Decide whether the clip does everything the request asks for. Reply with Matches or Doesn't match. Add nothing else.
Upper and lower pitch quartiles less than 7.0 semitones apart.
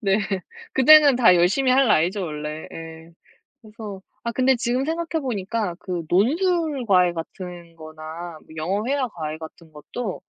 Doesn't match